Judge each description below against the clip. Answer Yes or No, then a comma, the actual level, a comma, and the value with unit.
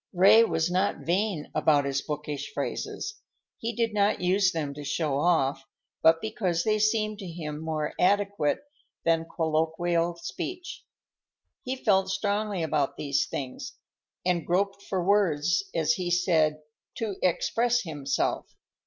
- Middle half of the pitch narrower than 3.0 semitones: No, average, 4.7 semitones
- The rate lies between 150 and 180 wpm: No, slow, 135 wpm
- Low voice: No, medium, 175 Hz